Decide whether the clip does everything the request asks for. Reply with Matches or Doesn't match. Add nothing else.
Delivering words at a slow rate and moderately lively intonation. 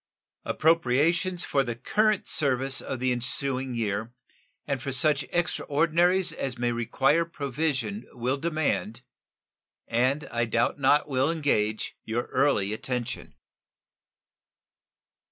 Matches